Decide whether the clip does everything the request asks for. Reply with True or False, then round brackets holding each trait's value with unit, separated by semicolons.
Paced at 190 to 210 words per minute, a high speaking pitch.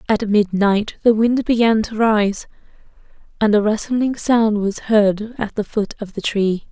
False (170 wpm; 215 Hz)